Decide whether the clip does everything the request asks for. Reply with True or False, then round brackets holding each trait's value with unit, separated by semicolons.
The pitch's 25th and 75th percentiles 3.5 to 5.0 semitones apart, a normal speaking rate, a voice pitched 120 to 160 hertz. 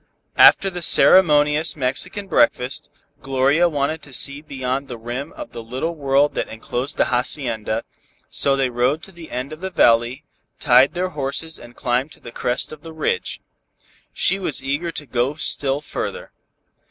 True (3.8 semitones; 165 wpm; 140 Hz)